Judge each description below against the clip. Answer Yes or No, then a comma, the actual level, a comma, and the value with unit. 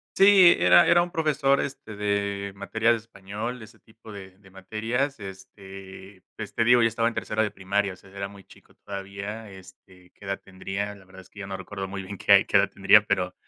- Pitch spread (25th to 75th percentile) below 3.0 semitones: Yes, narrow, 2.6 semitones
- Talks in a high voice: No, low, 100 Hz